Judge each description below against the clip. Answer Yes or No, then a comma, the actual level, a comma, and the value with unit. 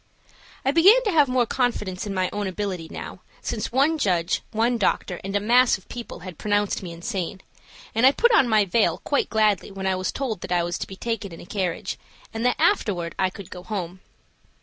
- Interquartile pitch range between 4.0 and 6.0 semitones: Yes, average, 4.8 semitones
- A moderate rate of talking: No, fast, 215 wpm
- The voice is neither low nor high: No, high, 205 Hz